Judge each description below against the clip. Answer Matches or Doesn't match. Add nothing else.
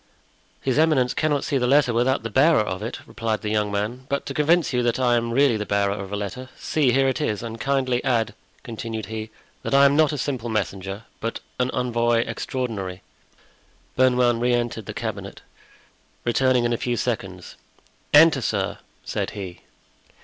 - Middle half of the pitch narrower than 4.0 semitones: Matches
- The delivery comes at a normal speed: Matches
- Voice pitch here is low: Matches